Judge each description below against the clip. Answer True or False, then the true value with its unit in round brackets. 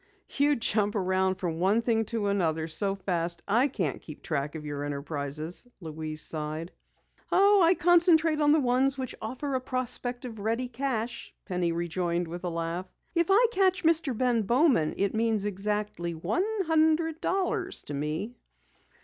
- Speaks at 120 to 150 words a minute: False (160 wpm)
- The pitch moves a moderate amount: False (8.2 semitones)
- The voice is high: True (210 Hz)